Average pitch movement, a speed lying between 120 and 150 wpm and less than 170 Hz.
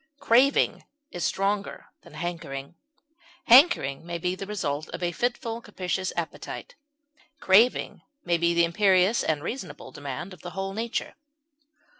No: average, 4.4 semitones; average, 140 wpm; medium, 185 Hz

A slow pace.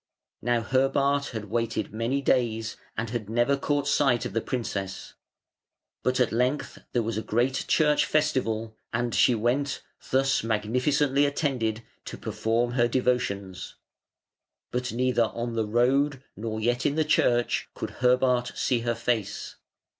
No: average, 145 wpm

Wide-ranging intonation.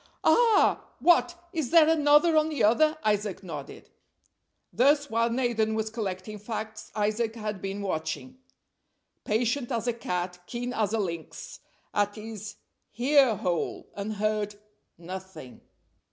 No: average, 4.0 semitones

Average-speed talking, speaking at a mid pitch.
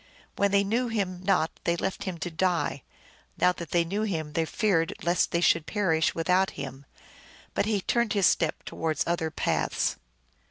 Yes: average, 175 wpm; medium, 180 Hz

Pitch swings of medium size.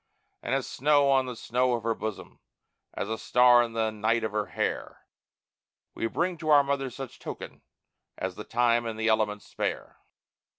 Yes: average, 3.2 semitones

